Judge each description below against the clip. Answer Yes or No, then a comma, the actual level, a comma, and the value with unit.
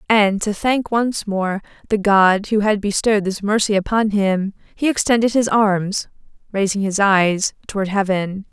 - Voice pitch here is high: Yes, high, 205 Hz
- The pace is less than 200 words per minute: Yes, average, 160 wpm